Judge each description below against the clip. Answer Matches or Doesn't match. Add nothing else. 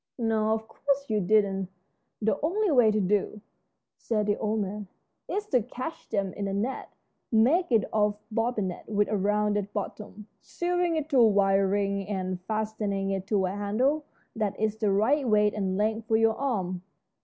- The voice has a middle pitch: Doesn't match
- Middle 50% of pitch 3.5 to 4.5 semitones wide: Doesn't match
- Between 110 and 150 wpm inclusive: Doesn't match